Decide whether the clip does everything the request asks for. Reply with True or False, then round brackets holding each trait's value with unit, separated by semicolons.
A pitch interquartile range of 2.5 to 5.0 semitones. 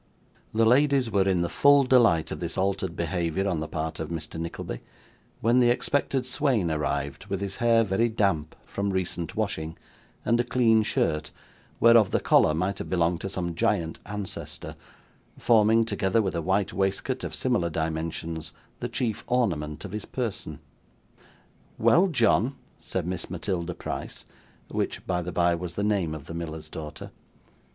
False (5.5 semitones)